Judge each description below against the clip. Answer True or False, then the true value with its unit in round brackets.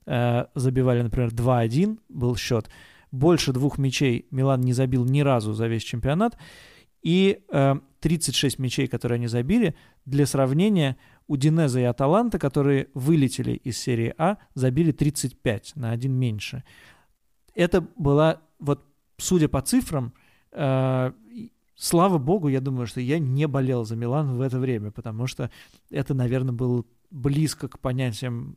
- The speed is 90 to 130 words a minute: False (140 wpm)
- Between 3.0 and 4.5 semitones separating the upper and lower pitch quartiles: True (3.4 semitones)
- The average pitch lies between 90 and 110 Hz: False (135 Hz)